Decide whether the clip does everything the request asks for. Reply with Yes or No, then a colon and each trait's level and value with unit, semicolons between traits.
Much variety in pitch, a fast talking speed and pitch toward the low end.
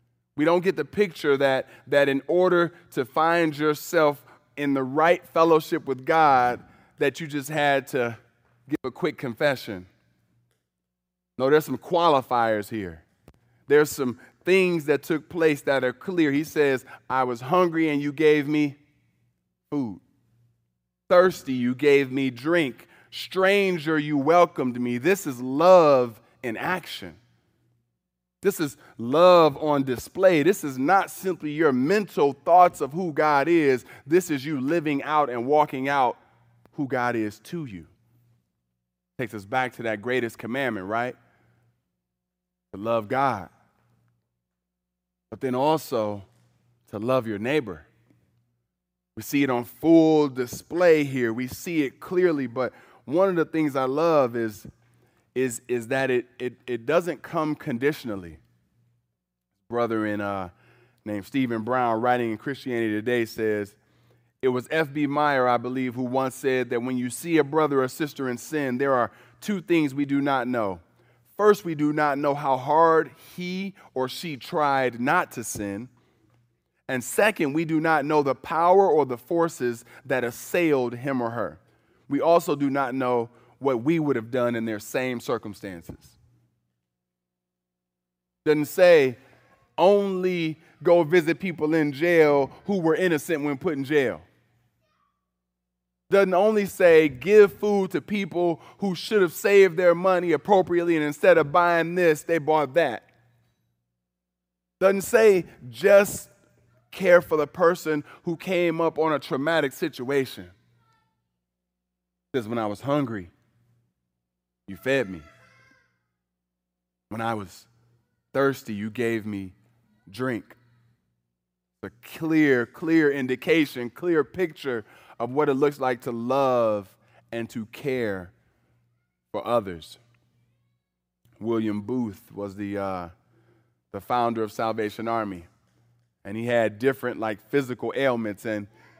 No: wide, 6.5 semitones; average, 140 wpm; low, 125 Hz